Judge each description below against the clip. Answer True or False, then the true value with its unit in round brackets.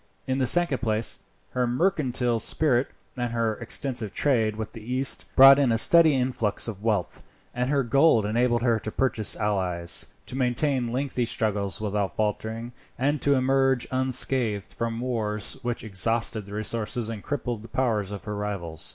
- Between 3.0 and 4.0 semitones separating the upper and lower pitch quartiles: True (3.4 semitones)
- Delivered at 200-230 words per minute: False (165 wpm)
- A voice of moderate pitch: False (120 Hz)